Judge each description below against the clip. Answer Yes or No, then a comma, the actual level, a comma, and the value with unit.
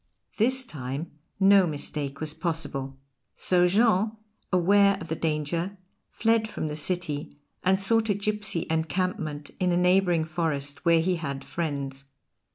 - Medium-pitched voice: Yes, medium, 170 Hz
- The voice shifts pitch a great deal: No, average, 4.5 semitones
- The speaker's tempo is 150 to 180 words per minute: No, average, 140 wpm